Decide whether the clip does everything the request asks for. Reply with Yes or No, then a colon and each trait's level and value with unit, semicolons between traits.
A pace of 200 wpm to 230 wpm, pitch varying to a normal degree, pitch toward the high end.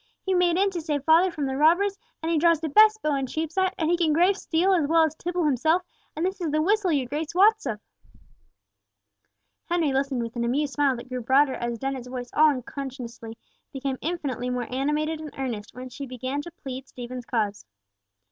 Yes: fast, 205 wpm; average, 4.7 semitones; very high, 295 Hz